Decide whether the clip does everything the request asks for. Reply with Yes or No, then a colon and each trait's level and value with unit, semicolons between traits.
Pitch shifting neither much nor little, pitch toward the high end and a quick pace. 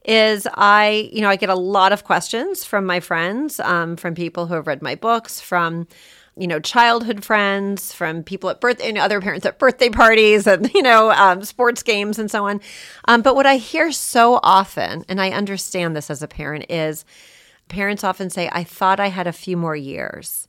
Yes: average, 4.3 semitones; high, 200 Hz; fast, 215 wpm